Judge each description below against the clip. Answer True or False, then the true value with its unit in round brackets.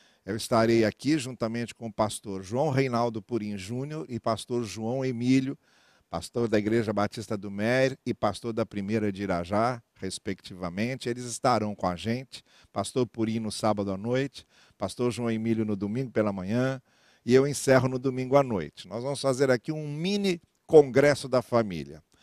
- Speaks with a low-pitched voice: True (115 Hz)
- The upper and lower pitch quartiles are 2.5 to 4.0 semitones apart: True (3.5 semitones)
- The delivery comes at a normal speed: True (165 wpm)